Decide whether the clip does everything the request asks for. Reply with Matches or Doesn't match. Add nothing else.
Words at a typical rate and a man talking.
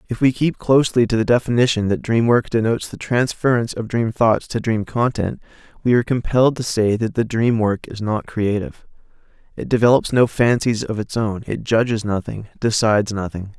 Matches